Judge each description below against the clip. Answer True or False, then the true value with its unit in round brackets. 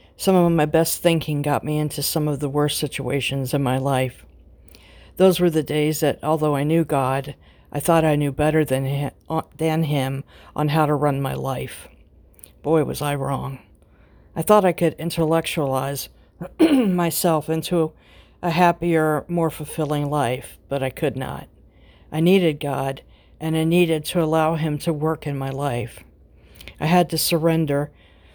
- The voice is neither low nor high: True (150 Hz)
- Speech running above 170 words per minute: False (160 wpm)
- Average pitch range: True (3.3 semitones)